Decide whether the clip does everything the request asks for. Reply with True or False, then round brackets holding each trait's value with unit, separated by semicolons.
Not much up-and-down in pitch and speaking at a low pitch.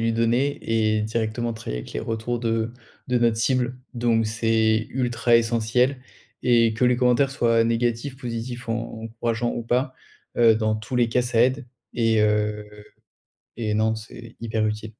True (1.5 semitones; 115 Hz)